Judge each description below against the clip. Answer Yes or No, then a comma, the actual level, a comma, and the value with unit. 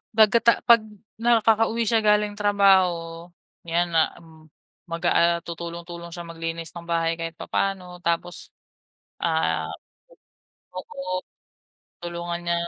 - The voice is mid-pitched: Yes, medium, 175 Hz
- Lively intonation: No, average, 3.5 semitones